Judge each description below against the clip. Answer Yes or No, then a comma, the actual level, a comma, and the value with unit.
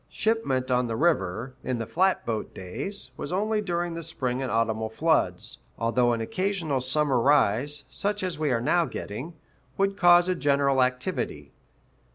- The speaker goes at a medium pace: Yes, average, 160 wpm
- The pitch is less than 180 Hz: Yes, medium, 140 Hz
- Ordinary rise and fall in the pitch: No, wide, 6.5 semitones